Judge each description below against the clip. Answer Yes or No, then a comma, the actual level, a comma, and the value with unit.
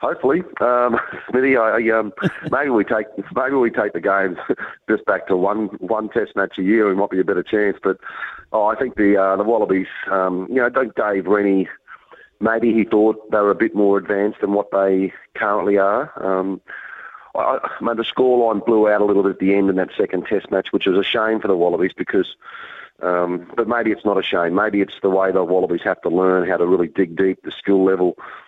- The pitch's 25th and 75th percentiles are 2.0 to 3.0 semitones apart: Yes, narrow, 2.4 semitones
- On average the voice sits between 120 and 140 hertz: No, low, 100 Hz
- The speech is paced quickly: Yes, fast, 230 wpm